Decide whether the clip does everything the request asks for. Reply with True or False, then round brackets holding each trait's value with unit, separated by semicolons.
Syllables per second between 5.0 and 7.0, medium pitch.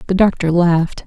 True (5.6 syllables/s; 175 Hz)